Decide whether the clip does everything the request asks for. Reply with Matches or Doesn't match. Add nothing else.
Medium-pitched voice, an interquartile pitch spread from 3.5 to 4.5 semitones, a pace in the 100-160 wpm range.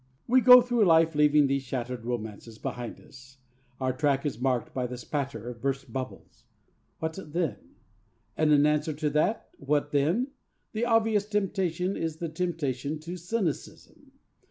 Doesn't match